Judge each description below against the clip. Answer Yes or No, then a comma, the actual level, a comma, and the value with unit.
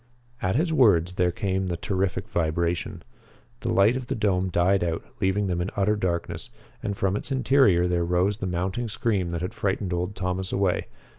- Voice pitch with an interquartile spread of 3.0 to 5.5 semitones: No, narrow, 2.6 semitones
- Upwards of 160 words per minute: Yes, average, 190 wpm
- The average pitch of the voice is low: Yes, very low, 95 Hz